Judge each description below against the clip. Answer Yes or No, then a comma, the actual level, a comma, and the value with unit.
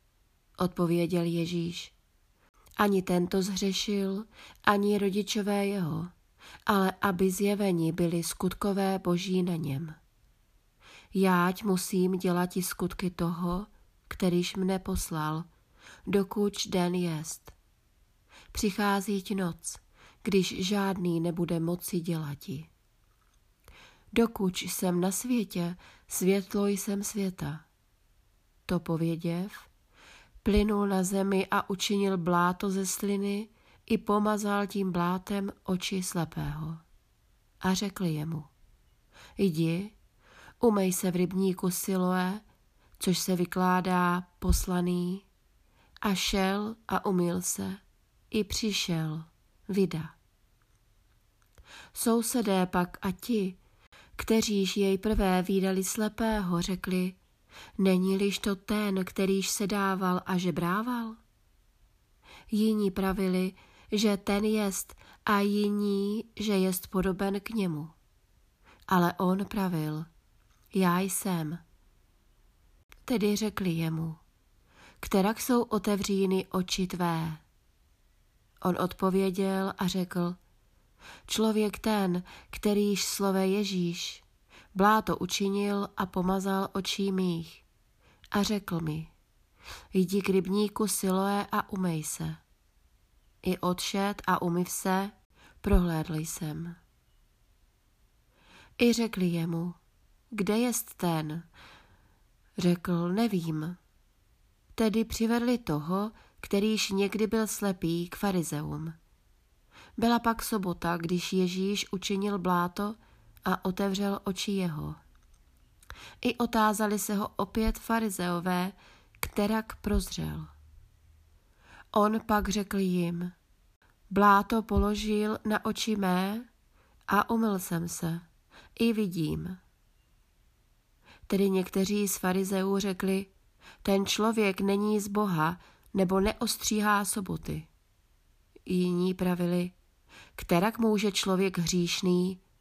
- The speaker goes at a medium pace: No, slow, 95 wpm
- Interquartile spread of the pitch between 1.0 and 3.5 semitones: Yes, average, 2.7 semitones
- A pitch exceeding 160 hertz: Yes, high, 190 Hz